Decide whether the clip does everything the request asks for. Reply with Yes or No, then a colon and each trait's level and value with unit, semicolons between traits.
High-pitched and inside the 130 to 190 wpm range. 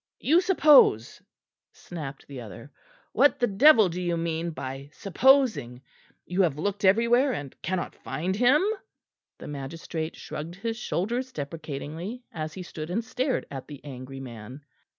No: medium, 170 Hz; average, 145 wpm